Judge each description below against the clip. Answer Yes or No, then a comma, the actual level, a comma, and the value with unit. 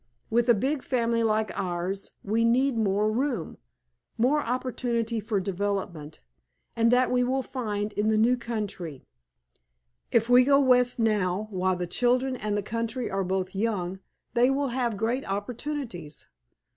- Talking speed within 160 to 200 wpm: No, average, 145 wpm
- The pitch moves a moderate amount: Yes, average, 3.9 semitones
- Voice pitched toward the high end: Yes, high, 225 Hz